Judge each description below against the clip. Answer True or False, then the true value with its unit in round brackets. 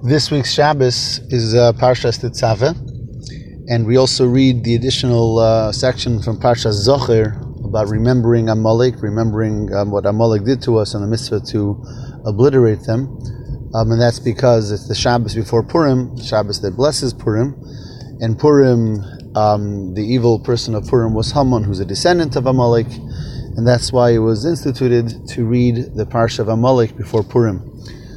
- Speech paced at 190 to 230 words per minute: False (160 wpm)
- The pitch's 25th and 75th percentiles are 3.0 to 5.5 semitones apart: False (2.4 semitones)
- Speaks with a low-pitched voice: True (120 Hz)